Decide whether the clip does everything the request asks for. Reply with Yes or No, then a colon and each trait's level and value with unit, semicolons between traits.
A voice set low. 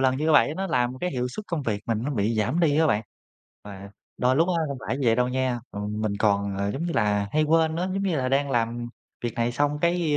Yes: low, 130 Hz